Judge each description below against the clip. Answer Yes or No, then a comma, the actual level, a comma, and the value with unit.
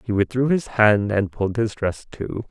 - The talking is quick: Yes, fast, 215 wpm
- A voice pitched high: No, low, 110 Hz